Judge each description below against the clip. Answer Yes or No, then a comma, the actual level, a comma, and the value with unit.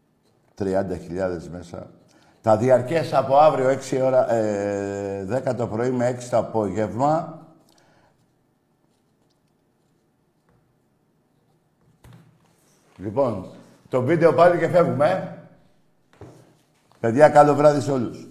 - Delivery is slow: Yes, slow, 90 wpm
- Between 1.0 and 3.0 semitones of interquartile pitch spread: No, wide, 5.8 semitones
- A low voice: Yes, low, 130 Hz